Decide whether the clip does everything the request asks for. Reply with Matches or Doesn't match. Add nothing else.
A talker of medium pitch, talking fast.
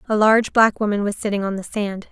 Doesn't match